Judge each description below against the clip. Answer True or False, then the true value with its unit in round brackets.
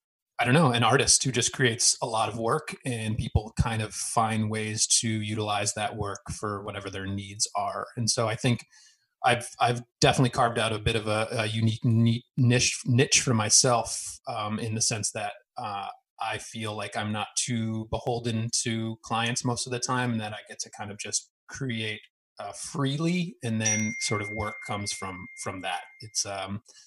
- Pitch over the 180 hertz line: False (115 Hz)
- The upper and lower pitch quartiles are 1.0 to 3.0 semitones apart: True (2.5 semitones)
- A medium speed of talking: True (195 wpm)